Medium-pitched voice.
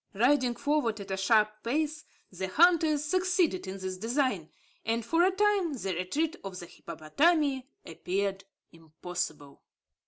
No: high, 230 Hz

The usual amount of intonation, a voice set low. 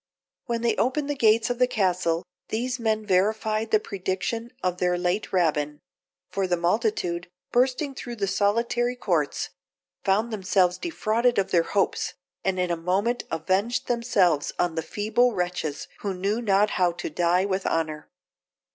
No: average, 4.6 semitones; high, 195 Hz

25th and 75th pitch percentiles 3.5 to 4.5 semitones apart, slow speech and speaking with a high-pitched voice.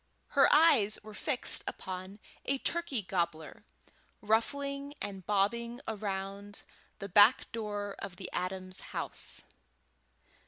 Yes: average, 3.9 semitones; slow, 110 wpm; high, 205 Hz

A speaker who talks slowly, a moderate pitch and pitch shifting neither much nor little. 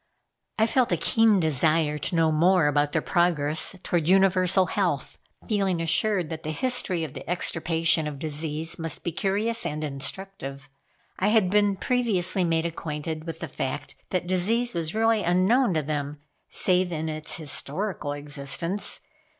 No: average, 155 wpm; medium, 170 Hz; average, 4.0 semitones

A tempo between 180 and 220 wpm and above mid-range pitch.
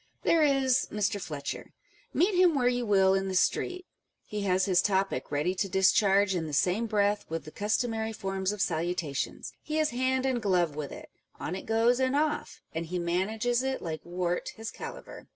Yes: average, 190 wpm; high, 200 Hz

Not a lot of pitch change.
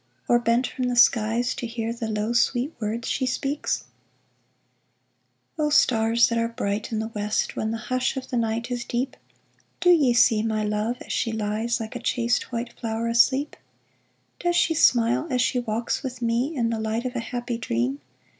Yes: narrow, 2.0 semitones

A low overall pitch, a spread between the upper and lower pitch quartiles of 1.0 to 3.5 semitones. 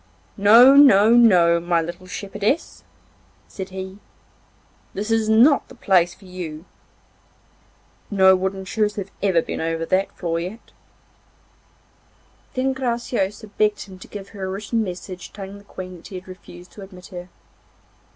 No: high, 195 Hz; average, 2.7 semitones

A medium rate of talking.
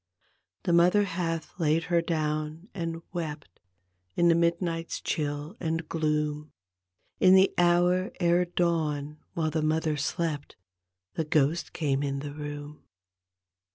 No: slow, 125 wpm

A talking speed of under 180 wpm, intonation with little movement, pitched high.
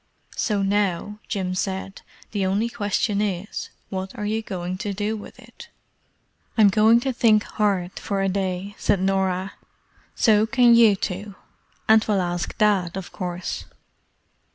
Yes: average, 150 wpm; narrow, 2.1 semitones; high, 200 Hz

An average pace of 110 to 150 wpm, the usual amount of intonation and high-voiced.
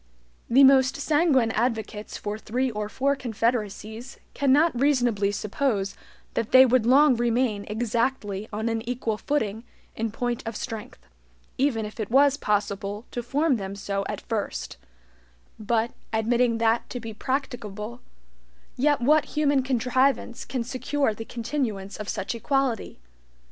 Yes: average, 140 wpm; average, 3.5 semitones; high, 235 Hz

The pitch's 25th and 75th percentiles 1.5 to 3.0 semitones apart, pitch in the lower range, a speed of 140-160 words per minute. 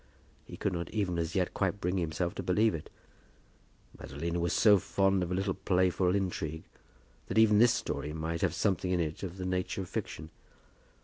No: narrow, 2.5 semitones; very low, 90 Hz; average, 190 wpm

